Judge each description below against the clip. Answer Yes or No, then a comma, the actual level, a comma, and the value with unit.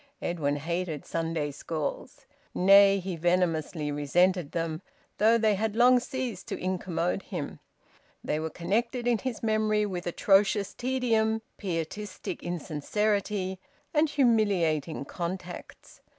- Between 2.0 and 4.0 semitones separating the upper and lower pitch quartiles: No, average, 4.6 semitones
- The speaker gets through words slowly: Yes, slow, 115 wpm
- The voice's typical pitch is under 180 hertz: No, medium, 185 Hz